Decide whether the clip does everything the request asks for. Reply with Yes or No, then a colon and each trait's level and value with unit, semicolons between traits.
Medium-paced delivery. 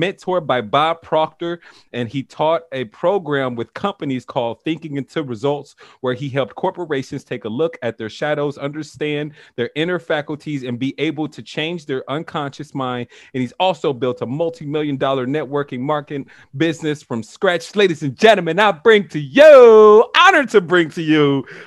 Yes: average, 165 wpm